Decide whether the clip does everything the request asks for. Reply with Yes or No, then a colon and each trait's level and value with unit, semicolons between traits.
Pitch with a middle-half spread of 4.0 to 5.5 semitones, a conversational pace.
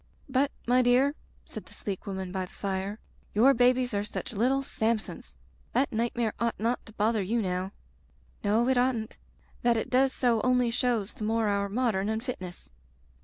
No: average, 3.6 semitones; average, 170 wpm